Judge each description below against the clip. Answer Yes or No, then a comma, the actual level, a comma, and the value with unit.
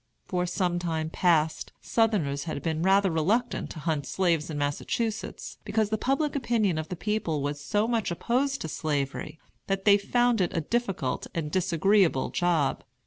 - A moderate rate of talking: Yes, average, 165 wpm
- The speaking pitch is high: No, medium, 180 Hz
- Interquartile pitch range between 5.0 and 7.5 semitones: Yes, wide, 5.4 semitones